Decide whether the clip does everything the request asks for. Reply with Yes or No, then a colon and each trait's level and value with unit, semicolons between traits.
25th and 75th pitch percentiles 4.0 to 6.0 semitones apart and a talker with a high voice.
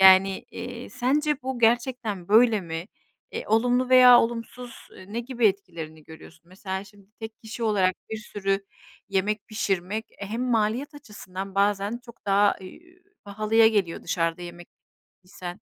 No: average, 3.5 semitones; high, 205 Hz